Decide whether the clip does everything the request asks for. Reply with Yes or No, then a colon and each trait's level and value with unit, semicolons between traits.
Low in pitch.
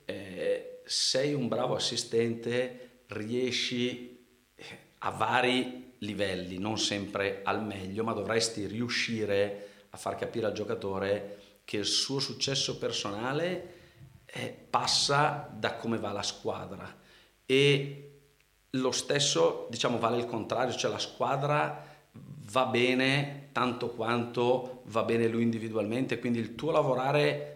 Yes: low, 120 Hz